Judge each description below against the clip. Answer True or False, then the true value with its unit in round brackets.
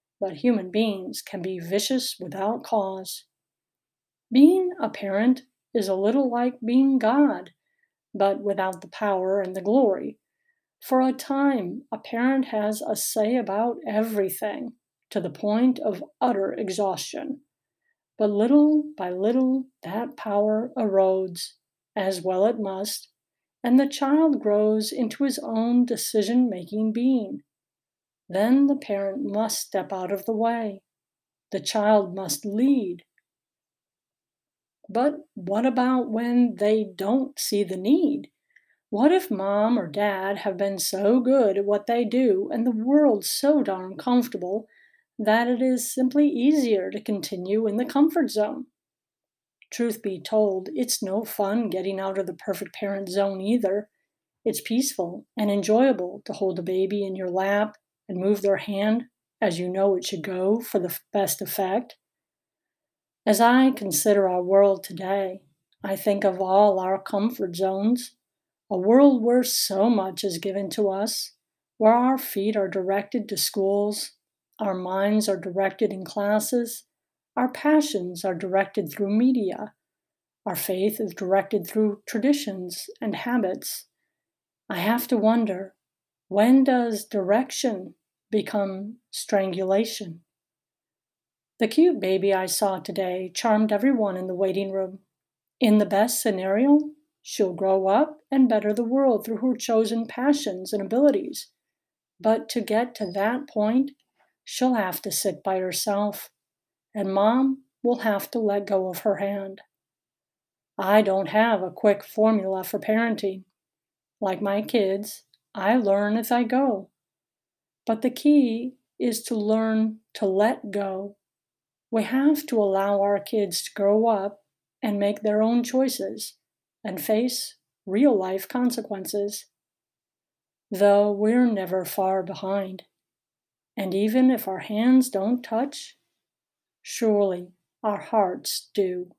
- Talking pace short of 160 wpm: True (140 wpm)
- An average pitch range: True (3.8 semitones)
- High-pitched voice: True (210 Hz)